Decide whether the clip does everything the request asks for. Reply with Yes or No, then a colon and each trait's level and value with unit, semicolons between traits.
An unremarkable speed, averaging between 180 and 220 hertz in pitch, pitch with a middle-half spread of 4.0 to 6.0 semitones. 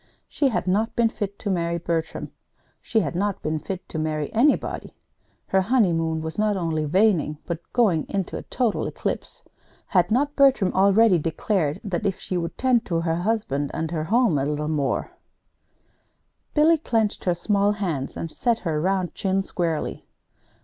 Yes: average, 170 wpm; medium, 185 Hz; average, 5.0 semitones